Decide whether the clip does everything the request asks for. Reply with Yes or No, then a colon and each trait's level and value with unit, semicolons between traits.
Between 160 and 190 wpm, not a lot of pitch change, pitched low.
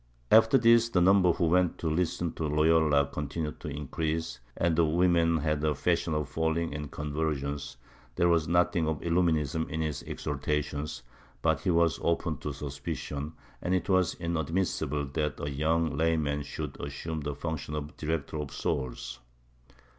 Yes: average, 165 wpm; narrow, 2.3 semitones; very low, 80 Hz